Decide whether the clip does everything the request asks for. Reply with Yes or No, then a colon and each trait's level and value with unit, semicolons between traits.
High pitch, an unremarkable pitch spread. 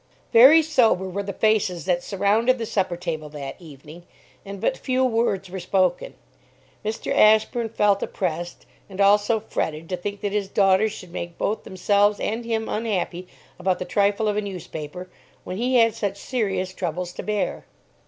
Yes: high, 200 Hz; average, 3.2 semitones